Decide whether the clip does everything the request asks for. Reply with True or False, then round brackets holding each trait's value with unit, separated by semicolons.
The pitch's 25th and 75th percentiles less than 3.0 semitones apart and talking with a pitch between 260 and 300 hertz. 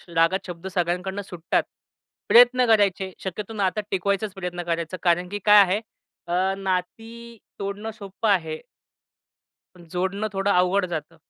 False (2.4 semitones; 190 Hz)